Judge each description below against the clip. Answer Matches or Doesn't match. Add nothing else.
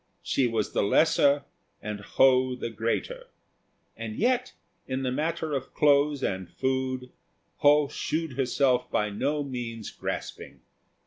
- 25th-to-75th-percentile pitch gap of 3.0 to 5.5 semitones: Matches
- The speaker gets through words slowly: Matches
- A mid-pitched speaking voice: Doesn't match